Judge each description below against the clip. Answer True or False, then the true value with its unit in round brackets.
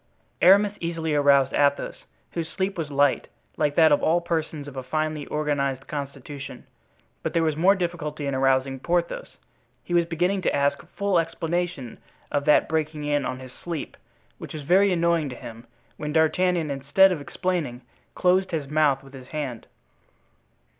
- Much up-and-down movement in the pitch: False (3.5 semitones)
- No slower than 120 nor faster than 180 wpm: True (165 wpm)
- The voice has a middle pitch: True (155 Hz)